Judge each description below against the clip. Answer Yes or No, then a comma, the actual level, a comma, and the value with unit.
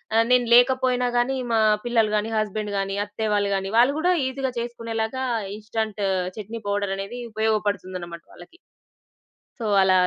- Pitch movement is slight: No, average, 3.0 semitones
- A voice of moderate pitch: No, high, 220 Hz